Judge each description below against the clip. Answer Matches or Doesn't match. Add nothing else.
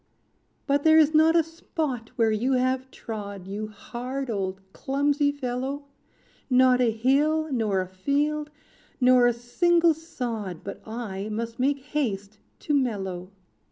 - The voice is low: Doesn't match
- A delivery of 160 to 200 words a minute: Doesn't match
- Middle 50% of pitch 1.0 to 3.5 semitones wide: Doesn't match